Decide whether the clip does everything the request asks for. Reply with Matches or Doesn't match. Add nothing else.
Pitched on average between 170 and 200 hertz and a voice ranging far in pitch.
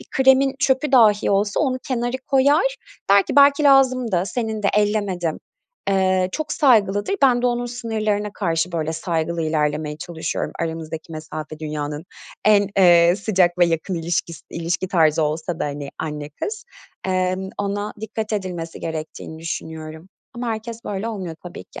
Matches